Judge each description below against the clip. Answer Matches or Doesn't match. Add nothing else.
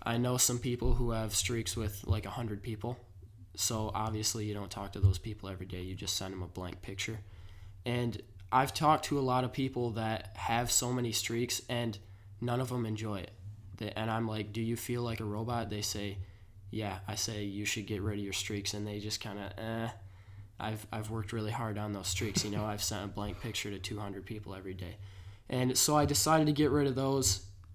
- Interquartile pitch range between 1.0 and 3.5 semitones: Matches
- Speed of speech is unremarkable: Doesn't match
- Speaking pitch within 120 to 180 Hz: Doesn't match